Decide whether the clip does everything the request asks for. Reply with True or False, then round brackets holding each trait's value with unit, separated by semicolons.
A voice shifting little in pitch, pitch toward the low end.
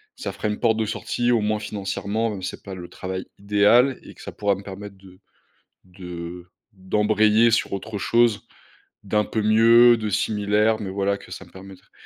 True (2.2 semitones; 105 Hz)